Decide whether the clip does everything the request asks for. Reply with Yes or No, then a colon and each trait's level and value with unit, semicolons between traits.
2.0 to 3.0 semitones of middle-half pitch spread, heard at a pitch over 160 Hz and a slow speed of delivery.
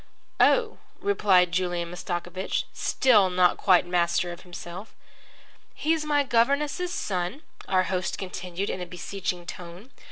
No: average, 4.9 semitones; medium, 185 Hz; slow, 125 wpm